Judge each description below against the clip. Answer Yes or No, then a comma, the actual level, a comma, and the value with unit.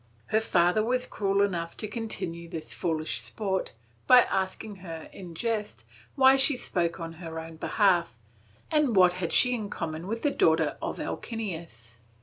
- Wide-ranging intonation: No, average, 4.9 semitones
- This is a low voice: No, medium, 185 Hz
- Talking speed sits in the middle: Yes, average, 160 wpm